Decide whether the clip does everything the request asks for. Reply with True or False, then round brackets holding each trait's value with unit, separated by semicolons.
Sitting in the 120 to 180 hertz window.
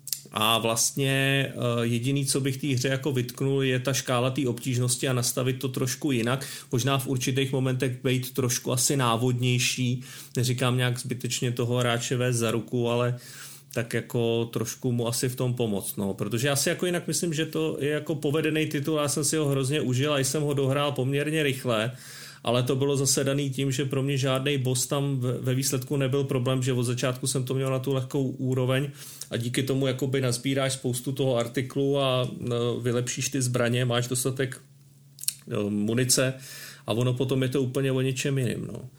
True (130 Hz)